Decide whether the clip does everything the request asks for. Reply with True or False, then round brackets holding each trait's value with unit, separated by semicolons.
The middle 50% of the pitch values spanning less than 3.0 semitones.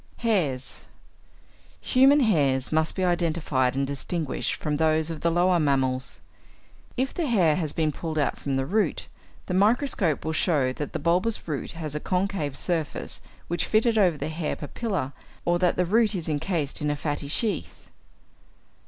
False (4.2 semitones)